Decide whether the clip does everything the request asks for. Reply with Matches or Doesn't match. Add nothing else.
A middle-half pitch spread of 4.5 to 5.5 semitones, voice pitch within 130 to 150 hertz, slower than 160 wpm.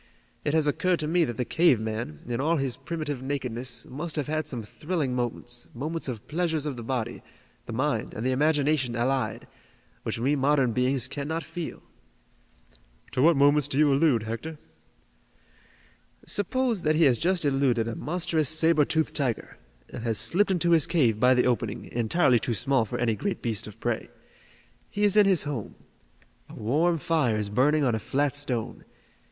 Doesn't match